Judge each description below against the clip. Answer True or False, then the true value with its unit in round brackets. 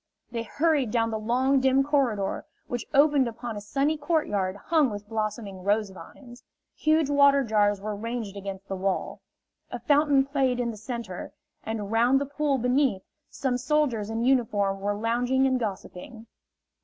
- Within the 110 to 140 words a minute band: False (160 wpm)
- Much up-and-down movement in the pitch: False (4.7 semitones)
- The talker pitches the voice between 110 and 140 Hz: False (235 Hz)